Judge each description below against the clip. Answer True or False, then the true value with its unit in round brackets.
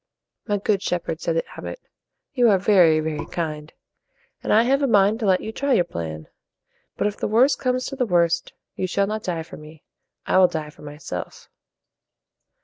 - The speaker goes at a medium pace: True (195 wpm)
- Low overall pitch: False (185 Hz)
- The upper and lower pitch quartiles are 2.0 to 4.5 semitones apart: False (5.4 semitones)